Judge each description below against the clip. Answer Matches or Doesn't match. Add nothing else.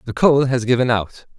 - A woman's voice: Doesn't match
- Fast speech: Matches